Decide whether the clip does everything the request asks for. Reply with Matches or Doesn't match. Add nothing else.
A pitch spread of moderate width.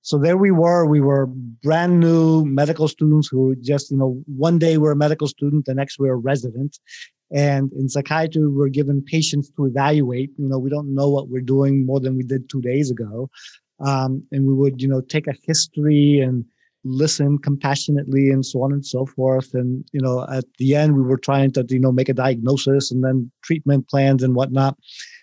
Doesn't match